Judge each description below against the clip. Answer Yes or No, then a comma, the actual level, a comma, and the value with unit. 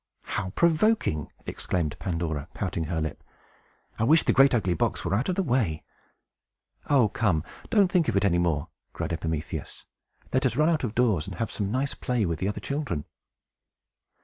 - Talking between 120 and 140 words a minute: No, average, 180 wpm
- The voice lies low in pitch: Yes, low, 100 Hz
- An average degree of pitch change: No, wide, 8.6 semitones